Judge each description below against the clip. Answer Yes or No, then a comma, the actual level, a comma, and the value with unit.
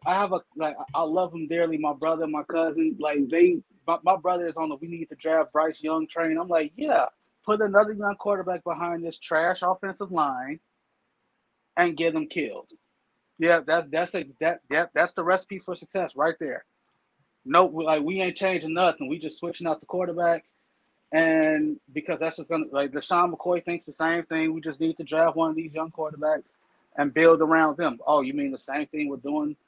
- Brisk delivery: Yes, fast, 210 wpm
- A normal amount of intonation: No, narrow, 2.2 semitones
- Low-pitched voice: No, medium, 165 Hz